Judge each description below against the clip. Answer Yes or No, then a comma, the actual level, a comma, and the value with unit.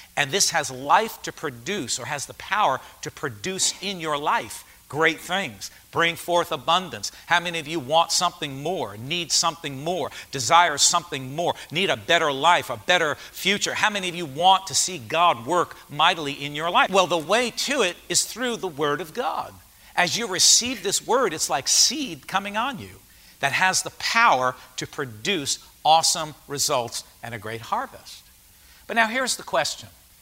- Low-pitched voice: No, medium, 170 Hz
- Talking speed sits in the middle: Yes, average, 185 wpm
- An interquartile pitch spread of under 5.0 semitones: Yes, average, 4.6 semitones